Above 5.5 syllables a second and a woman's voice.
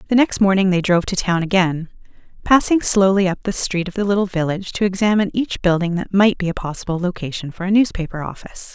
Yes: 6.4 syllables/s; female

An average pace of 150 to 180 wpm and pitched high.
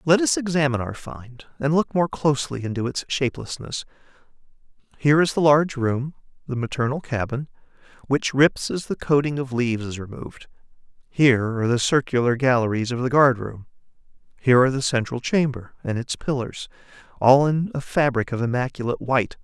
No: average, 165 wpm; low, 130 Hz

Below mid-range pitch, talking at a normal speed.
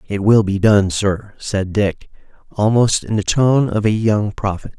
Yes: low, 105 Hz; average, 190 wpm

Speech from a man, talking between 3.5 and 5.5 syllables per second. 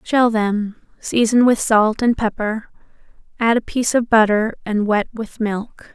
No: female; 4.2 syllables/s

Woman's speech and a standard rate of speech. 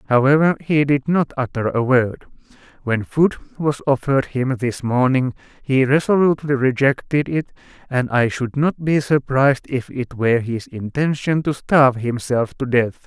No: male; average, 155 wpm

